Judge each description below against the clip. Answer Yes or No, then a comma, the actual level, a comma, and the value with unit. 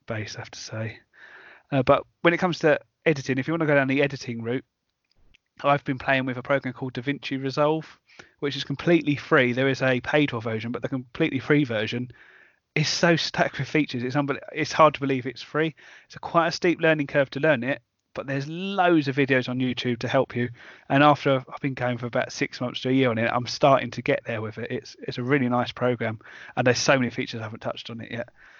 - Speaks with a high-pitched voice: No, low, 135 Hz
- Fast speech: Yes, fast, 240 wpm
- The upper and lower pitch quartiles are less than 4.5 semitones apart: Yes, average, 3.0 semitones